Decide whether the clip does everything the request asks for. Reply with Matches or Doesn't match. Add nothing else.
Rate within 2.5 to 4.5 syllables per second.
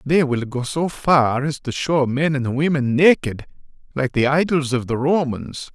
Matches